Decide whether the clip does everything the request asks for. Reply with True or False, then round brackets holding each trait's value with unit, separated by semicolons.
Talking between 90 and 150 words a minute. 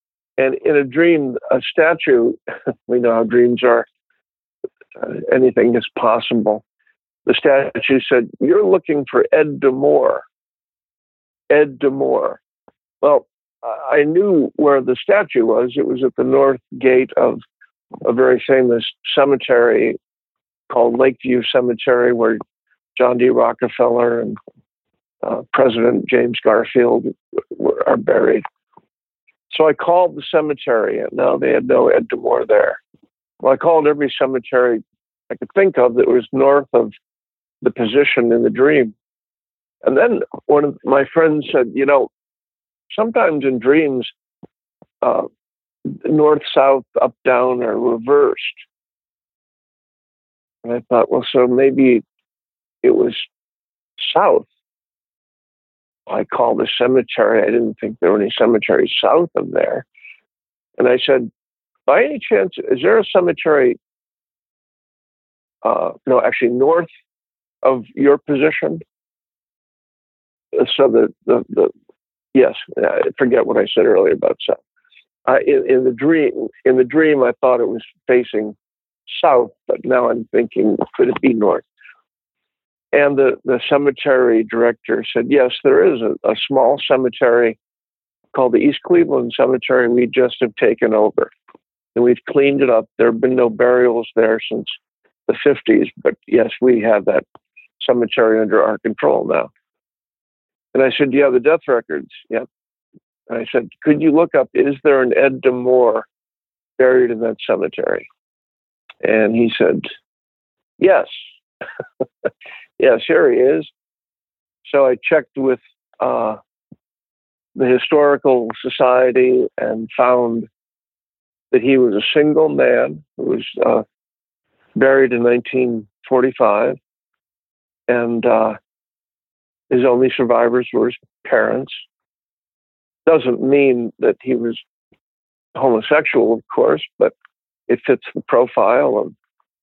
True (135 wpm)